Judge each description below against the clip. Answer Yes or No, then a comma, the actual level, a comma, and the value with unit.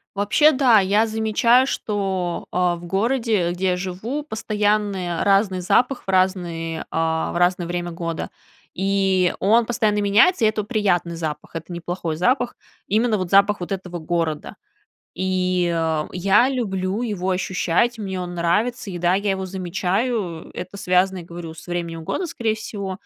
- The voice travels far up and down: No, average, 3.4 semitones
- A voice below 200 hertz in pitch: Yes, high, 190 Hz